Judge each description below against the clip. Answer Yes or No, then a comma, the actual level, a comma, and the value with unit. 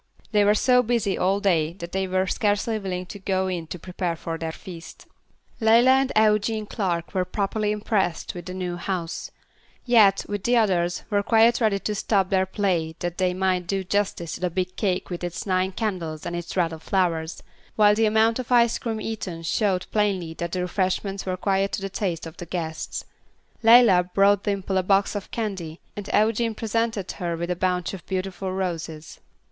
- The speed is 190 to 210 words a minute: Yes, average, 195 wpm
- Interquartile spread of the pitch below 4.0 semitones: Yes, average, 3.0 semitones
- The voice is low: No, high, 190 Hz